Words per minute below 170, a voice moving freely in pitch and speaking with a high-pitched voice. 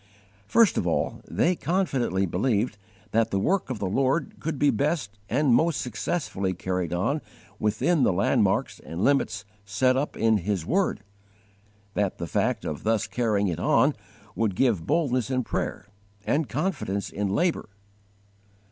No: average, 150 wpm; wide, 6.8 semitones; low, 115 Hz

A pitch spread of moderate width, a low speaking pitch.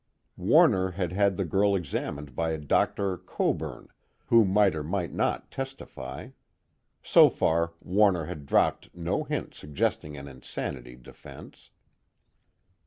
Yes: average, 4.9 semitones; very low, 85 Hz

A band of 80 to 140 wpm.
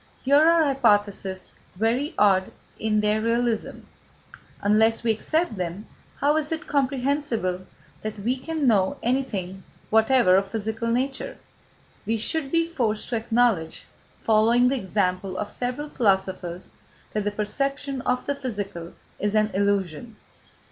Yes: slow, 135 wpm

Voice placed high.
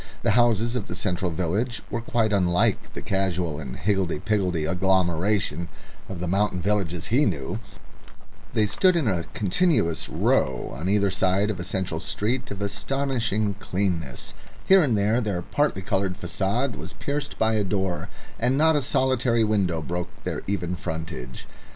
No: low, 100 Hz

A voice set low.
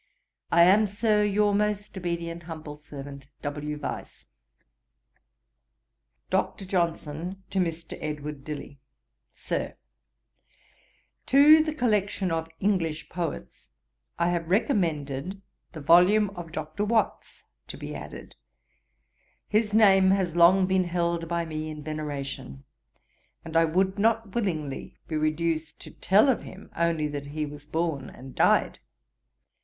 No: medium, 170 Hz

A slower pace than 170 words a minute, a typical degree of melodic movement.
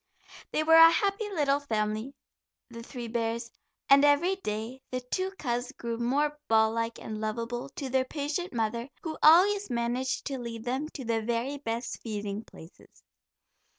Yes: average, 160 wpm; average, 4.1 semitones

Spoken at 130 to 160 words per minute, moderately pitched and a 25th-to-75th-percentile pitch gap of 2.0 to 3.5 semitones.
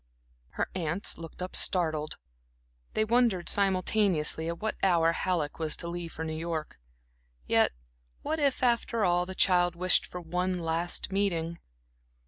Yes: average, 145 wpm; medium, 175 Hz; average, 2.7 semitones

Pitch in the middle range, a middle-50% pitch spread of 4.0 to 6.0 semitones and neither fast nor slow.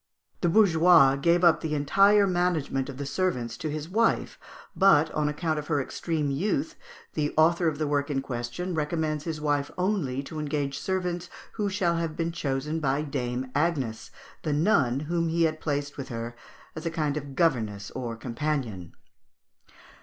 No: medium, 150 Hz; average, 3.5 semitones; average, 170 wpm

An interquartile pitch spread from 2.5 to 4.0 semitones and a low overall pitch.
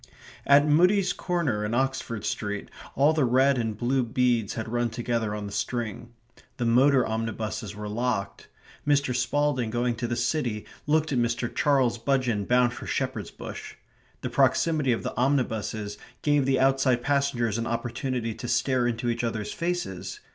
Yes: average, 3.2 semitones; low, 120 Hz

